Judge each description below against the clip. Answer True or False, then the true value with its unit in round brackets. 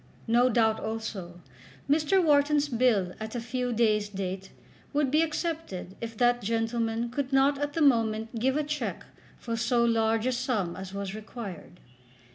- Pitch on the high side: True (235 Hz)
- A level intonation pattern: False (3.8 semitones)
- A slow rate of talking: False (160 wpm)